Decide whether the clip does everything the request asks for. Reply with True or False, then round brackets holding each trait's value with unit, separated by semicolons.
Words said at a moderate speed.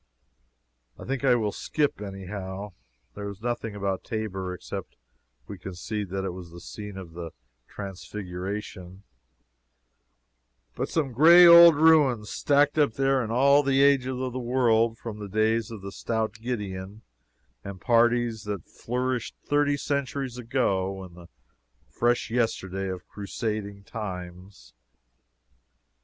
False (130 wpm)